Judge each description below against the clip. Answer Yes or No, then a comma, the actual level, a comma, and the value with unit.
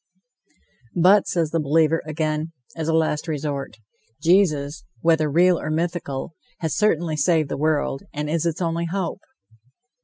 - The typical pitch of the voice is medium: Yes, medium, 160 Hz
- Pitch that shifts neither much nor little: No, narrow, 1.9 semitones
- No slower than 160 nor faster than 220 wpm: No, average, 145 wpm